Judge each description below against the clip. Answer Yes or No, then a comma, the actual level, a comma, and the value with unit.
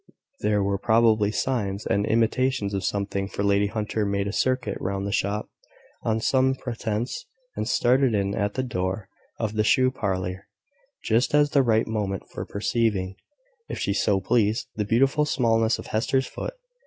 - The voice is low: Yes, low, 110 Hz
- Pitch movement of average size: Yes, average, 3.1 semitones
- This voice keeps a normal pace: Yes, average, 165 wpm